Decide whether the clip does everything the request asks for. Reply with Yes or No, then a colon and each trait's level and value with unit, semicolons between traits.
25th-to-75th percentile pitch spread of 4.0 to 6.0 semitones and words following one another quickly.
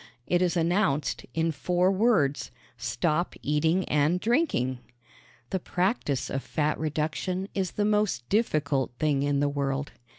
No: average, 4.6 semitones; slow, 135 wpm